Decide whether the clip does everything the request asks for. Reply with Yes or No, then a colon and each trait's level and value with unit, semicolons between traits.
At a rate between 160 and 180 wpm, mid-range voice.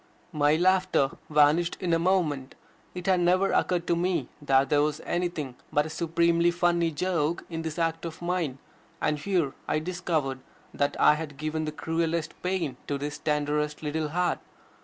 Yes: average, 170 wpm; medium, 160 Hz